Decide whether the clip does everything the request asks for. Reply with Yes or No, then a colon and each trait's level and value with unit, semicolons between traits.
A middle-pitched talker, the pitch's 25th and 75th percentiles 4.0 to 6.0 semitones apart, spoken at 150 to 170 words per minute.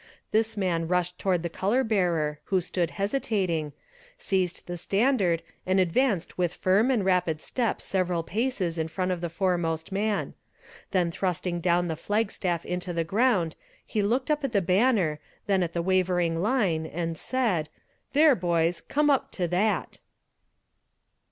No: medium, 180 Hz; average, 3.6 semitones; average, 160 wpm